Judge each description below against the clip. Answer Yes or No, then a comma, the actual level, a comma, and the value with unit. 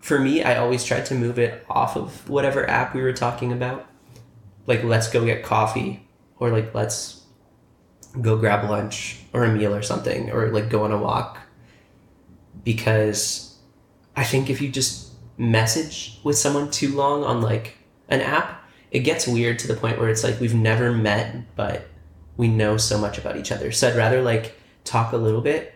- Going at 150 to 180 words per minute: No, average, 190 wpm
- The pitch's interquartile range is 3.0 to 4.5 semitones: No, narrow, 2.5 semitones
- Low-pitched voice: Yes, low, 115 Hz